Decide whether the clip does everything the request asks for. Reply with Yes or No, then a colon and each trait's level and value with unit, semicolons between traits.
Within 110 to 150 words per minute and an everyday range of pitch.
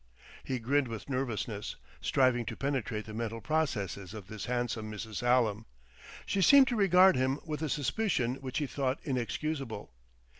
No: average, 160 wpm; average, 4.7 semitones